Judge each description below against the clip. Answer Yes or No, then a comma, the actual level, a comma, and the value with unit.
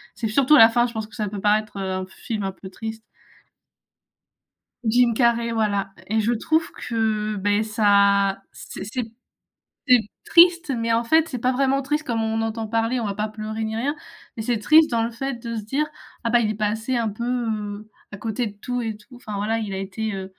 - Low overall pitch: No, high, 225 Hz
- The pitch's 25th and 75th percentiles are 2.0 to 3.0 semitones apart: Yes, narrow, 2.4 semitones